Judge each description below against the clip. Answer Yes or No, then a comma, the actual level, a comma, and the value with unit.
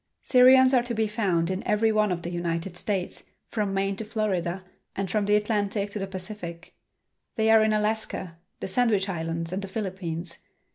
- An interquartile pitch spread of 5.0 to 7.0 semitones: No, average, 3.3 semitones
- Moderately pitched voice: No, high, 200 Hz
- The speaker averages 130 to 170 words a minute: No, average, 185 wpm